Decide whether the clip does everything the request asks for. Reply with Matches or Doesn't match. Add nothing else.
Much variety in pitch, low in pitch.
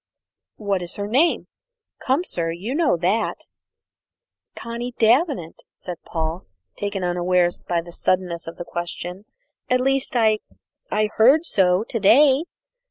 Doesn't match